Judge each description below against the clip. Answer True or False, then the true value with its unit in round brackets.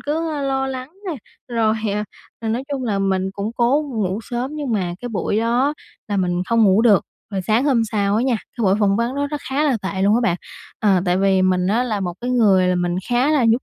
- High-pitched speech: True (225 Hz)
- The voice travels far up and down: False (4.7 semitones)